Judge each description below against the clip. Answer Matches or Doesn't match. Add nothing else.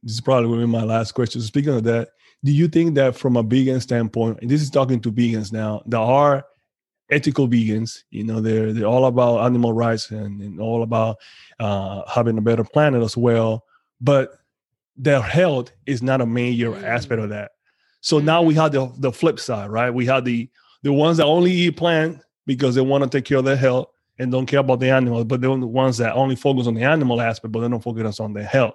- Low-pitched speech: Matches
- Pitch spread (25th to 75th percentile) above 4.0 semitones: Doesn't match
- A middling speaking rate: Doesn't match